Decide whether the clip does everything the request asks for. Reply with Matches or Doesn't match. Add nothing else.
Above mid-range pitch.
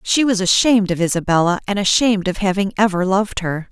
Matches